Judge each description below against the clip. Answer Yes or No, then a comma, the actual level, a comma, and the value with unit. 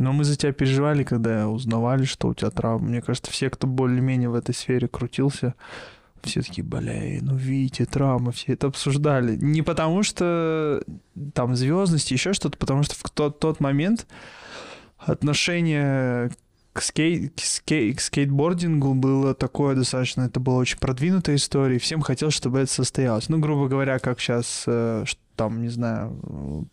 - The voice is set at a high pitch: No, low, 135 Hz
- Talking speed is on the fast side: Yes, fast, 165 wpm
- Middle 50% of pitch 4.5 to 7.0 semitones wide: No, average, 3.1 semitones